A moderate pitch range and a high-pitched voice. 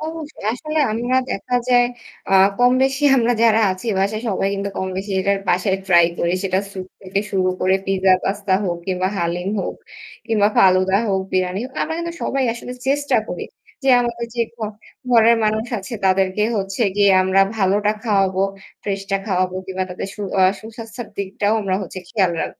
Yes: average, 3.7 semitones; high, 200 Hz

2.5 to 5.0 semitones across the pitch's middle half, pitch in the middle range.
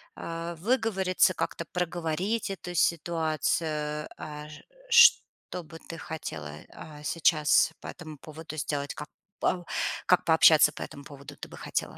Yes: average, 2.8 semitones; medium, 165 Hz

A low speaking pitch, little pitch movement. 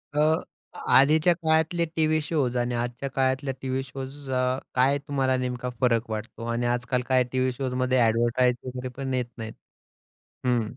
Yes: low, 130 Hz; narrow, 2.1 semitones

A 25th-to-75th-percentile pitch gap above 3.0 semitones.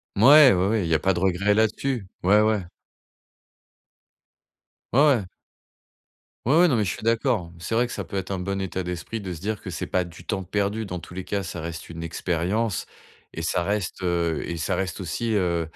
Yes: average, 3.7 semitones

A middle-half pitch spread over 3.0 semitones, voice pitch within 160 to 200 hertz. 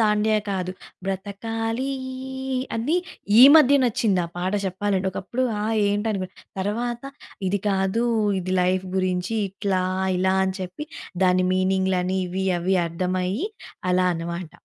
No: average, 2.7 semitones; high, 190 Hz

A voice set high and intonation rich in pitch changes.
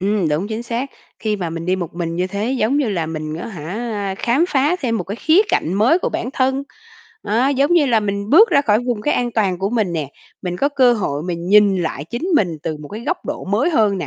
Yes: high, 210 Hz; wide, 6.0 semitones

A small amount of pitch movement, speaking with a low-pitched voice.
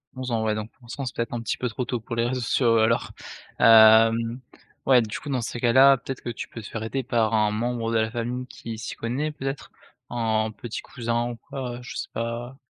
Yes: narrow, 1.8 semitones; low, 115 Hz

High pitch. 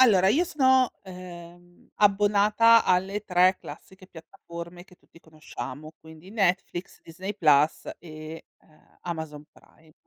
No: medium, 180 Hz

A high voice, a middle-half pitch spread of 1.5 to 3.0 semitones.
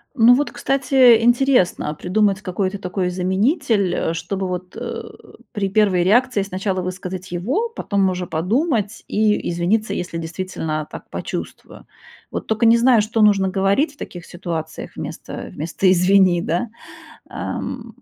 No: high, 195 Hz; average, 3.9 semitones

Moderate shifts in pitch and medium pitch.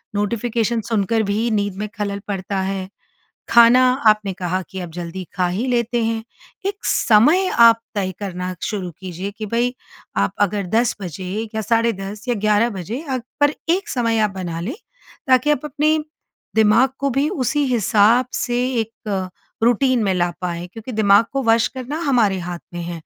No: average, 4.0 semitones; high, 215 Hz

